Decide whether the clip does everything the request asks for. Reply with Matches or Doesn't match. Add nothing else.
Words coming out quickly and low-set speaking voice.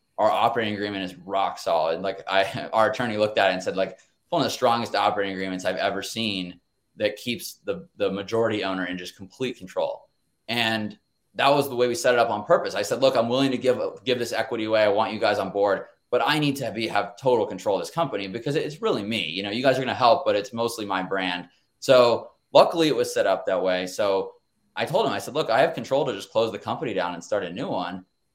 Matches